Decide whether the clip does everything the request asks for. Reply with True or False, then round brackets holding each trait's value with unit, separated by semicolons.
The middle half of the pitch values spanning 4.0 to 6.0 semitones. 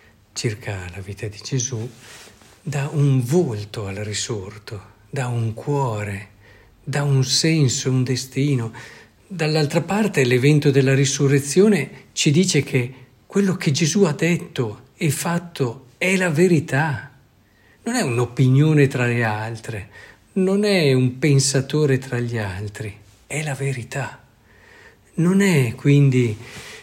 True (4.9 semitones)